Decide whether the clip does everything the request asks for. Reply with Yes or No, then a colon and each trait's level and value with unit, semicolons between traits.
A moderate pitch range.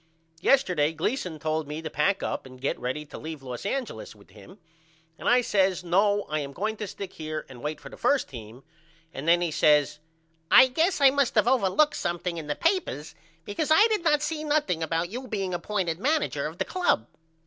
No: wide, 9.0 semitones